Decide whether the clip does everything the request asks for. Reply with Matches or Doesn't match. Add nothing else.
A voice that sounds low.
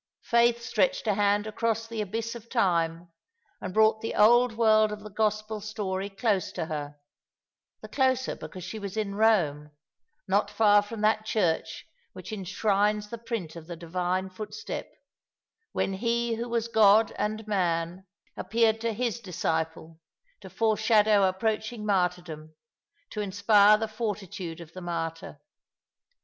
Doesn't match